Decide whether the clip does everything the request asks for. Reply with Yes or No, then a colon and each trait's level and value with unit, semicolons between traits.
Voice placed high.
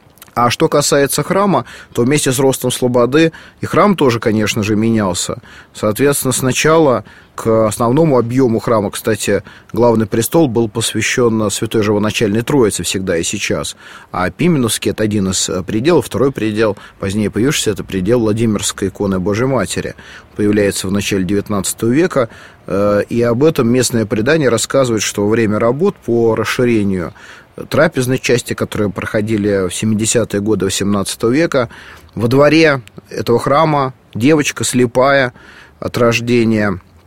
No: low, 115 Hz